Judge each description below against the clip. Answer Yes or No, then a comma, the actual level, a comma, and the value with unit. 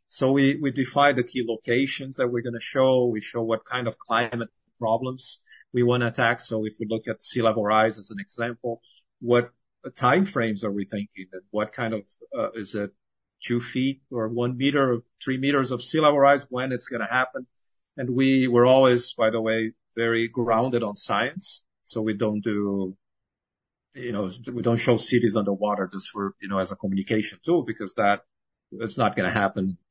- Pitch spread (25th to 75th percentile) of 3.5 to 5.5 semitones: No, average, 2.9 semitones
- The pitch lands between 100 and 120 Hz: Yes, low, 115 Hz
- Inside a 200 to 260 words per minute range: Yes, fast, 205 wpm